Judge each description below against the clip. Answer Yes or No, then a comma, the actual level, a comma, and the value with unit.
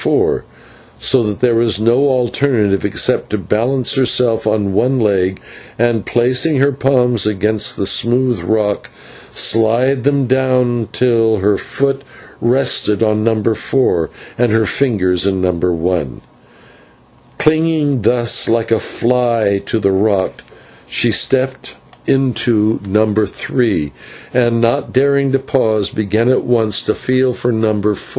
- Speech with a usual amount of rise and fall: Yes, average, 3.4 semitones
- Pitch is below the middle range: Yes, low, 115 Hz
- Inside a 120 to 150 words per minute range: Yes, average, 140 wpm